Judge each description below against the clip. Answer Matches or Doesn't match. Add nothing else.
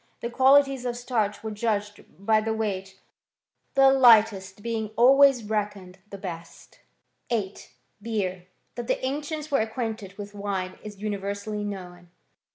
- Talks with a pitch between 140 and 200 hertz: Doesn't match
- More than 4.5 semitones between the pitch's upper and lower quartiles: Doesn't match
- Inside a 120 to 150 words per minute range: Matches